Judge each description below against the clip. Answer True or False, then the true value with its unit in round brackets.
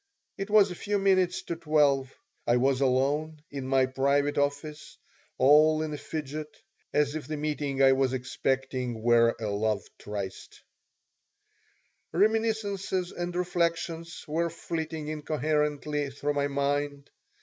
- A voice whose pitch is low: False (150 Hz)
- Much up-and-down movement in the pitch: False (3.5 semitones)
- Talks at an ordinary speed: False (130 wpm)